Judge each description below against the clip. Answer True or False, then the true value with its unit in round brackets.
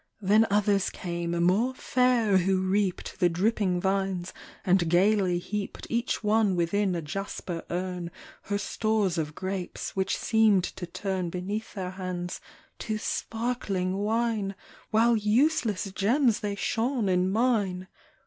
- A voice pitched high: True (195 Hz)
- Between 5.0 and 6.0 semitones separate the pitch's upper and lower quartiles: False (3.1 semitones)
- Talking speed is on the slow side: True (130 wpm)